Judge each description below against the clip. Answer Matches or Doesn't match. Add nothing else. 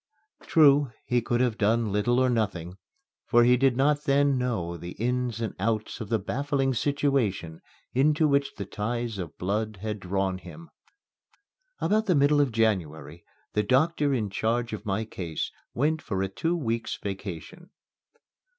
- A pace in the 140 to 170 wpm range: Matches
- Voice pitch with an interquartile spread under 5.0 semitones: Doesn't match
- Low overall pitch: Matches